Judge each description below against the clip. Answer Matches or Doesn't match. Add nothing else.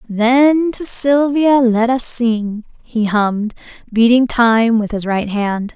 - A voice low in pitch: Doesn't match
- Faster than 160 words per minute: Doesn't match